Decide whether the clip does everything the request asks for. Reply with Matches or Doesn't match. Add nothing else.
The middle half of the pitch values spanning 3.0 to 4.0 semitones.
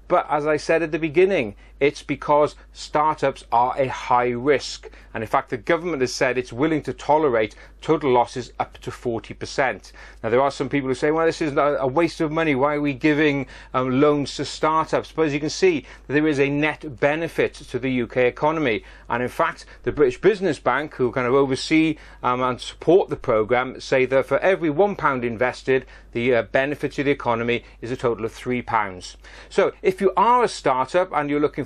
Matches